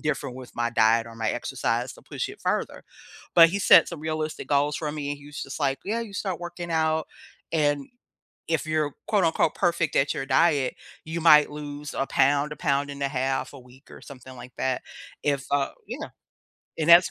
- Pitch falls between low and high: Yes, medium, 145 Hz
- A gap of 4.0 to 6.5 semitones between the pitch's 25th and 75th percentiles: No, average, 2.8 semitones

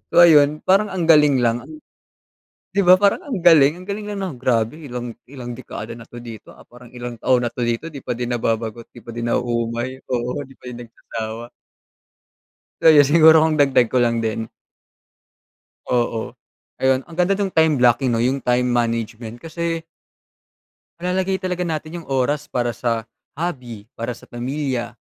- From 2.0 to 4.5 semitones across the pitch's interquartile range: No, average, 5.0 semitones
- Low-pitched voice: Yes, low, 125 Hz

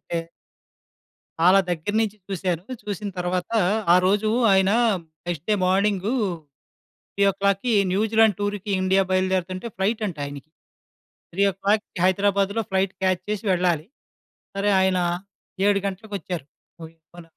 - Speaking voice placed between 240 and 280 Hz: No, high, 190 Hz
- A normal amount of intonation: No, narrow, 2.1 semitones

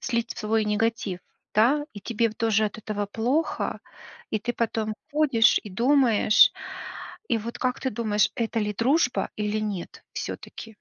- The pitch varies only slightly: Yes, narrow, 2.0 semitones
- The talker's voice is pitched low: No, high, 225 Hz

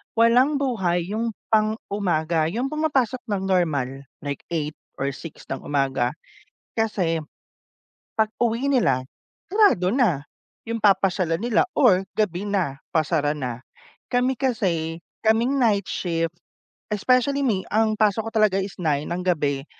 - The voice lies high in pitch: Yes, high, 195 Hz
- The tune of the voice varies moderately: No, wide, 6.0 semitones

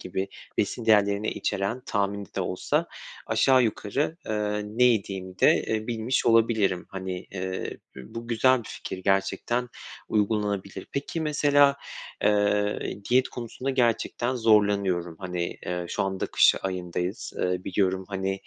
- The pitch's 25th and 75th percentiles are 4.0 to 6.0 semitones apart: No, average, 3.6 semitones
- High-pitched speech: No, low, 105 Hz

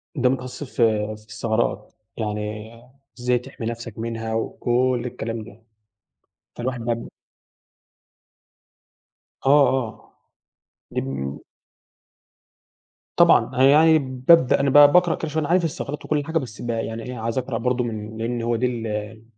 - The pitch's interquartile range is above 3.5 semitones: No, average, 2.8 semitones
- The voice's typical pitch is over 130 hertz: No, low, 120 Hz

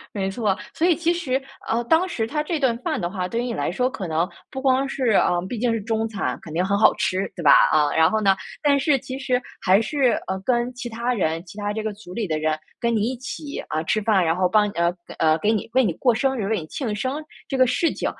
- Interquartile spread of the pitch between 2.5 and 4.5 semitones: No, average, 5.2 semitones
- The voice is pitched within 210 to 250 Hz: Yes, high, 220 Hz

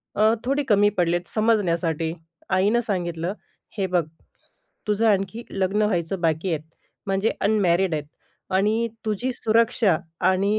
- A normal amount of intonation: Yes, average, 3.8 semitones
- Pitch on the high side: Yes, high, 195 Hz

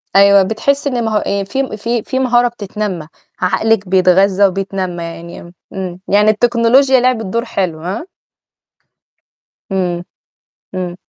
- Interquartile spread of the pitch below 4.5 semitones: Yes, average, 4.1 semitones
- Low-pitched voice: No, high, 200 Hz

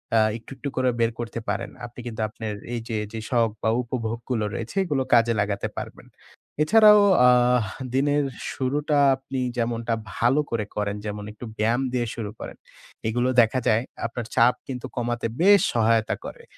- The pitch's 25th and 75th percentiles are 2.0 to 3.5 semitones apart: Yes, narrow, 2.4 semitones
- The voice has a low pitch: Yes, low, 120 Hz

